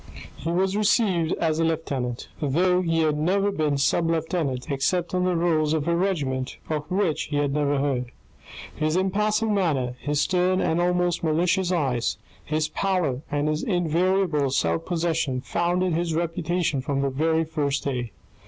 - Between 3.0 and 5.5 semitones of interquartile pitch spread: Yes, average, 3.7 semitones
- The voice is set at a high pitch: No, medium, 160 Hz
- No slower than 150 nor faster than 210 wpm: Yes, average, 160 wpm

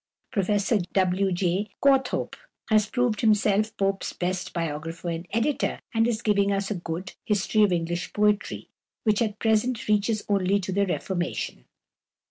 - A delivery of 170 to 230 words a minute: No, average, 145 wpm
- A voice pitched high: Yes, high, 200 Hz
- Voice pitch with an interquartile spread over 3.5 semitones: No, average, 2.8 semitones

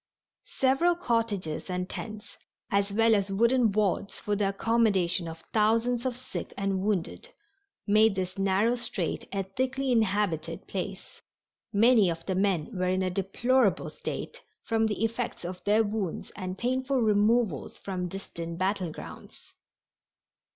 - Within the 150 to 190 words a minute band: No, average, 140 wpm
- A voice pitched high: Yes, high, 205 Hz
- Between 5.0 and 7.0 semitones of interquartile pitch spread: No, average, 3.6 semitones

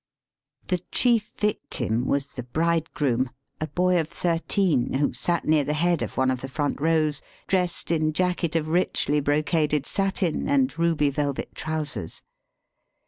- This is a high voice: No, medium, 155 Hz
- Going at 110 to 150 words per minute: Yes, average, 145 wpm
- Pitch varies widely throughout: No, average, 3.6 semitones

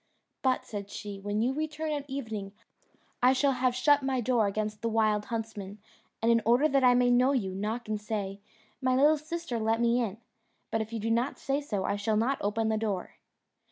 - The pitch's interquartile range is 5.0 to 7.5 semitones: No, average, 3.6 semitones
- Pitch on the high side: Yes, high, 230 Hz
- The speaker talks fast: Yes, fast, 210 wpm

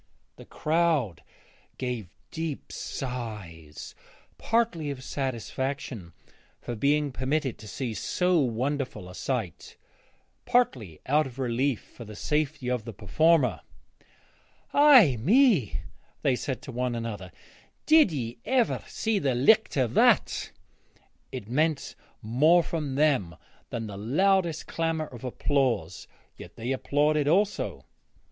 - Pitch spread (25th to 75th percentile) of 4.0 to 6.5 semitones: Yes, average, 5.2 semitones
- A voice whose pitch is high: No, low, 135 Hz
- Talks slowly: Yes, slow, 120 wpm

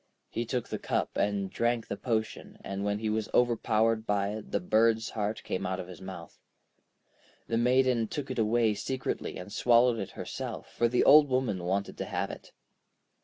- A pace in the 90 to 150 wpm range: No, average, 185 wpm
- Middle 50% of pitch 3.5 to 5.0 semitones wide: No, average, 2.9 semitones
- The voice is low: Yes, low, 110 Hz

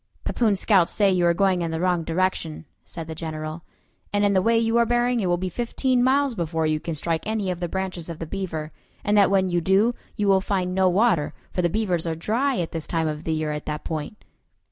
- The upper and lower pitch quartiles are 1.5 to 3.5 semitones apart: No, average, 4.1 semitones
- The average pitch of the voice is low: No, medium, 185 Hz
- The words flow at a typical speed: No, fast, 245 wpm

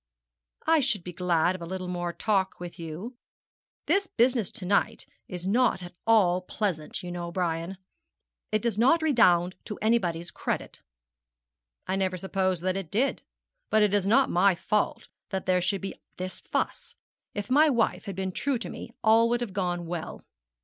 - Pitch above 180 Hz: Yes, high, 190 Hz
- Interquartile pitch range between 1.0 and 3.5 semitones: No, average, 4.0 semitones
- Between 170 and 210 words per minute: Yes, average, 180 wpm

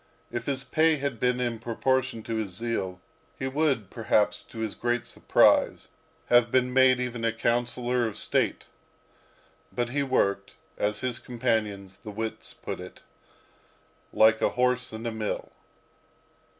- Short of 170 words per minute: Yes, average, 150 wpm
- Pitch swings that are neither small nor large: No, narrow, 2.3 semitones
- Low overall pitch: Yes, low, 120 Hz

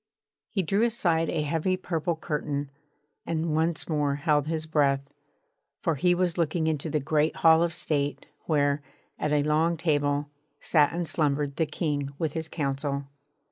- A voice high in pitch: No, medium, 155 Hz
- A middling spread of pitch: No, narrow, 2.2 semitones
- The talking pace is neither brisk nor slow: Yes, average, 160 wpm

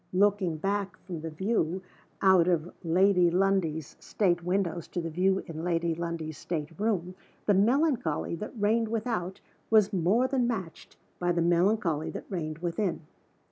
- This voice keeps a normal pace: Yes, average, 150 wpm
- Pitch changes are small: No, average, 3.3 semitones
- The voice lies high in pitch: No, medium, 180 Hz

